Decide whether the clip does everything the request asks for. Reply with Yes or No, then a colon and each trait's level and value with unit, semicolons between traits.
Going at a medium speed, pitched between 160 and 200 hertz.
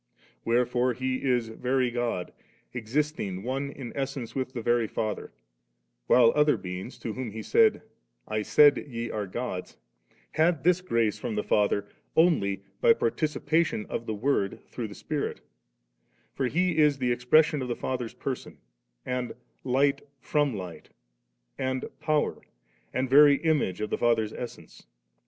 No: average, 155 wpm; low, 125 Hz